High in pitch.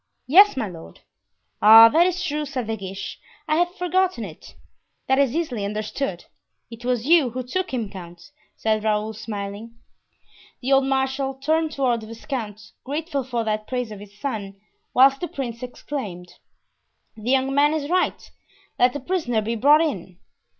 Yes: very high, 250 Hz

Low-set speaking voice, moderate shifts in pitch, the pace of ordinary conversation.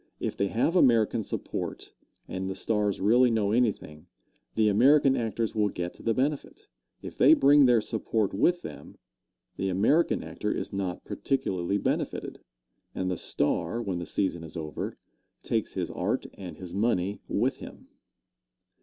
Yes: low, 105 Hz; average, 4.2 semitones; average, 155 wpm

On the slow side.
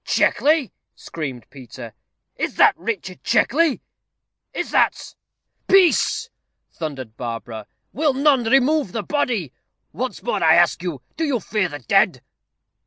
Yes: slow, 130 wpm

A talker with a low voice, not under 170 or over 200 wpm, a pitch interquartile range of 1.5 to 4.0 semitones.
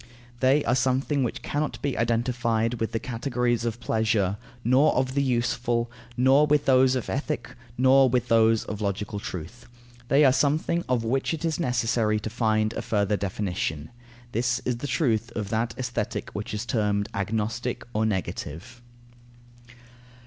No: low, 120 Hz; average, 155 wpm; average, 3.0 semitones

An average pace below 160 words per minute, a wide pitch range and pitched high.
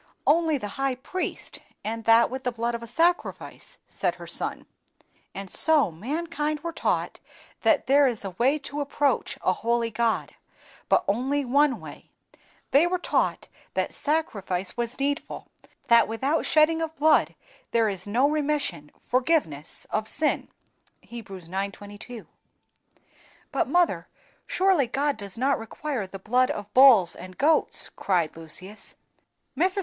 Yes: average, 145 wpm; wide, 6.3 semitones; very high, 250 Hz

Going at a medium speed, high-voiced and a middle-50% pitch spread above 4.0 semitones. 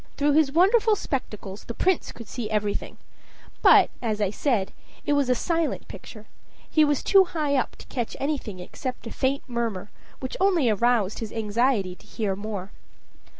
Yes: average, 170 wpm; high, 245 Hz; wide, 5.6 semitones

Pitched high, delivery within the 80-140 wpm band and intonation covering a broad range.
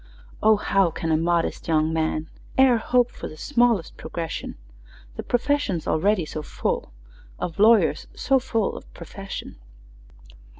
Yes: high, 195 Hz; slow, 135 wpm; wide, 6.4 semitones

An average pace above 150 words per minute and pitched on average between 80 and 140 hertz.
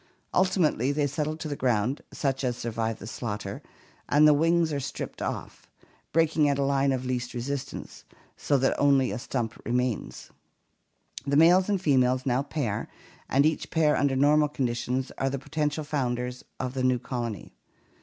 Yes: average, 175 wpm; low, 135 Hz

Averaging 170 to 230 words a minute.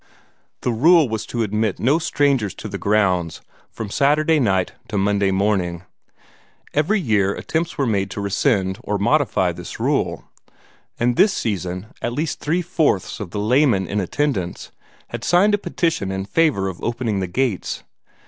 No: average, 160 wpm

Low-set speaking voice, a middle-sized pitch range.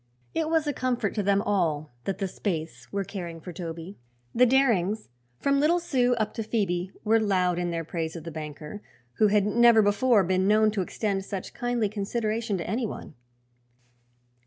No: high, 205 Hz; average, 4.5 semitones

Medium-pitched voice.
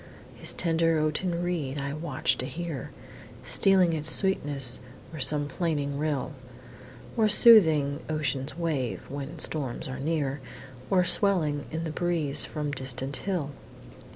Yes: medium, 155 Hz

